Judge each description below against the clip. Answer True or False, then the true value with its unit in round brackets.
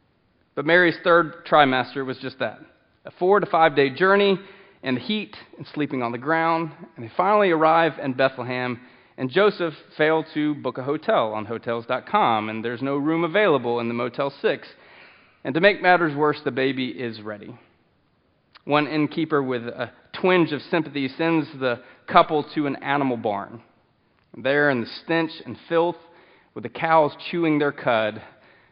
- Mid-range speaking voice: True (145 Hz)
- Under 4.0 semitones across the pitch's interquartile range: False (4.7 semitones)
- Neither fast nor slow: True (165 wpm)